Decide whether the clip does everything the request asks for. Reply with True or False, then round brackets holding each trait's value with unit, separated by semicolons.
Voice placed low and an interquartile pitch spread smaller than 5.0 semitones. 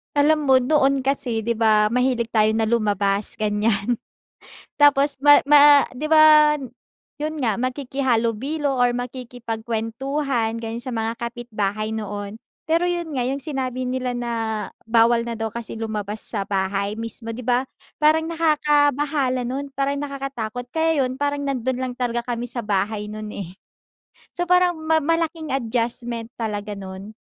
False (245 Hz; 4.2 semitones)